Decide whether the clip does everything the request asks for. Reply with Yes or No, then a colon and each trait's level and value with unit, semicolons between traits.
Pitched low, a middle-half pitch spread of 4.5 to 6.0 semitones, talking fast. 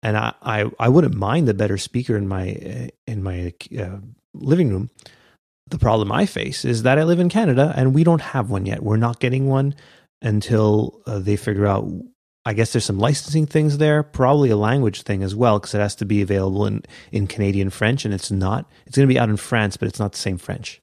Yes: low, 110 Hz; average, 5.0 semitones; fast, 230 wpm